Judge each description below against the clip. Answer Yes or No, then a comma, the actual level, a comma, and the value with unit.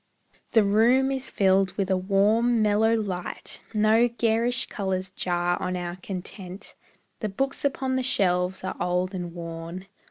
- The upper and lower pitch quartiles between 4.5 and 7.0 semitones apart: No, average, 3.9 semitones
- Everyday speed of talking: Yes, average, 150 wpm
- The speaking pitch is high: Yes, high, 195 Hz